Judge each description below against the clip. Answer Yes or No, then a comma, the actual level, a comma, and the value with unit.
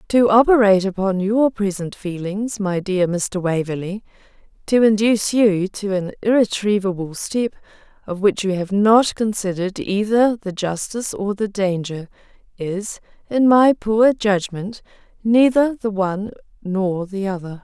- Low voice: No, high, 200 Hz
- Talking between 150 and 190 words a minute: No, slow, 135 wpm